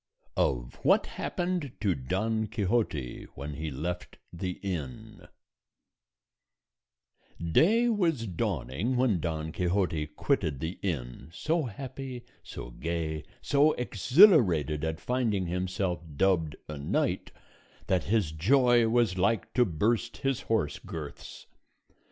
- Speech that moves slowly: Yes, slow, 115 wpm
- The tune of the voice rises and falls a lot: Yes, wide, 7.6 semitones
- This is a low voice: Yes, very low, 95 Hz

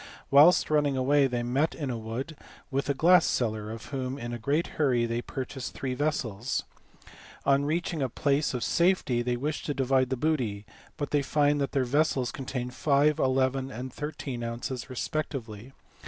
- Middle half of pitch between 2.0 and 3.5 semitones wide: Yes, average, 3.1 semitones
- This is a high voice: No, low, 135 Hz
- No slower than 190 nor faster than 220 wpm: No, average, 175 wpm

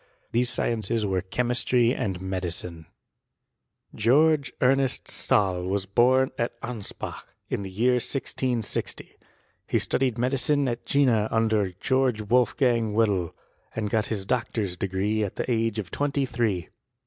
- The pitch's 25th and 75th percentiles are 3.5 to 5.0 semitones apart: Yes, average, 4.0 semitones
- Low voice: Yes, low, 115 Hz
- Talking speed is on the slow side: Yes, slow, 130 wpm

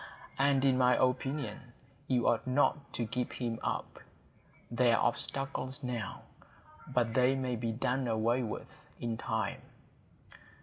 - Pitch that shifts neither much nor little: No, narrow, 2.0 semitones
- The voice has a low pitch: Yes, low, 125 Hz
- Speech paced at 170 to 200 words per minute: No, slow, 135 wpm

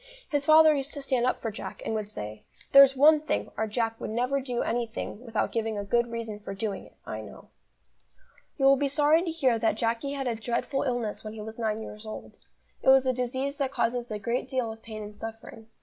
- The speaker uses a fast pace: Yes, fast, 230 wpm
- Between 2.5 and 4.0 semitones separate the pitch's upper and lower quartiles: Yes, average, 3.6 semitones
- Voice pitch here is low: No, high, 235 Hz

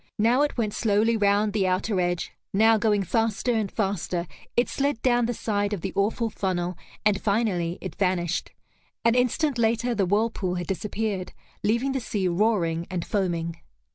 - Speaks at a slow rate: No, average, 170 wpm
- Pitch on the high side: Yes, high, 205 Hz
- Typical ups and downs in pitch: Yes, average, 3.6 semitones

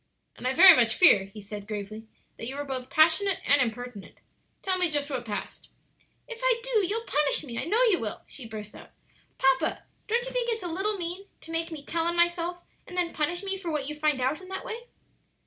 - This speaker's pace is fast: Yes, fast, 230 wpm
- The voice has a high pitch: Yes, very high, 325 Hz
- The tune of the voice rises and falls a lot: Yes, wide, 6.9 semitones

